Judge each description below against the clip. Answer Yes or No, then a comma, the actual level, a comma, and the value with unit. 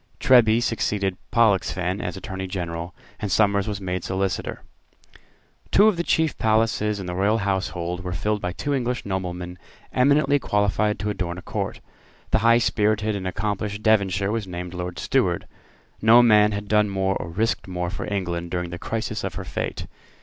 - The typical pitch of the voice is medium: No, low, 100 Hz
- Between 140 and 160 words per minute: No, average, 170 wpm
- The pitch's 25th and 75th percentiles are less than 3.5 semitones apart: Yes, average, 3.1 semitones